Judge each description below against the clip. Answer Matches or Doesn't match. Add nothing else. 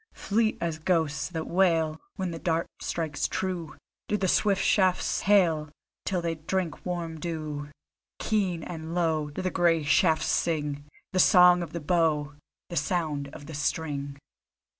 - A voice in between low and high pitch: Matches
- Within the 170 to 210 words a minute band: Doesn't match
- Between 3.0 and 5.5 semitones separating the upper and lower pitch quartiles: Doesn't match